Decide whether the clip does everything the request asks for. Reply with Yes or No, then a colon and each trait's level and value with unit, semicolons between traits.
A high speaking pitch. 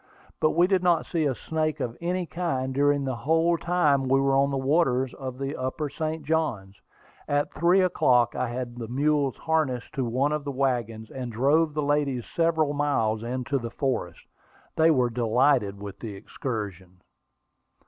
No: low, 135 Hz